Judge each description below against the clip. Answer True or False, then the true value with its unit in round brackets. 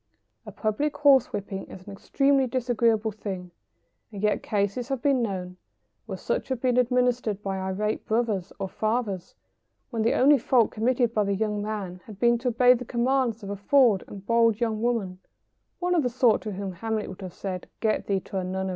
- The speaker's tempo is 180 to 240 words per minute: True (200 wpm)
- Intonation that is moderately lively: True (3.8 semitones)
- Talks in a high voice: True (220 Hz)